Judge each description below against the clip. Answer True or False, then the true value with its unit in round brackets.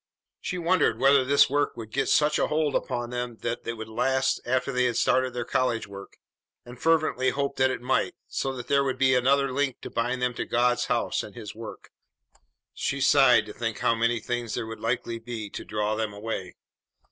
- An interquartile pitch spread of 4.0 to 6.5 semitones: False (2.6 semitones)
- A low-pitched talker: True (125 Hz)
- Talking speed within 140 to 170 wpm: False (205 wpm)